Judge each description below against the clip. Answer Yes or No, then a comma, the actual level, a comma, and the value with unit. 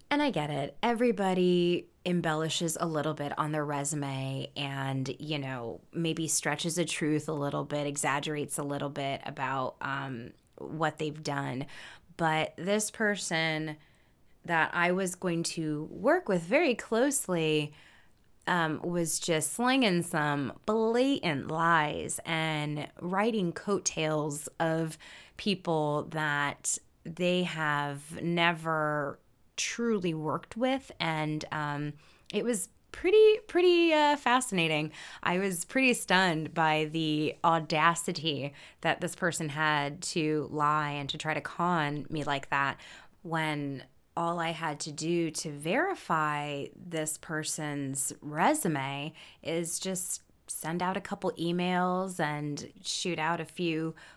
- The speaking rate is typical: No, slow, 125 wpm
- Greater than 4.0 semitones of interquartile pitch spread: No, average, 3.2 semitones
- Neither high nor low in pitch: Yes, medium, 160 Hz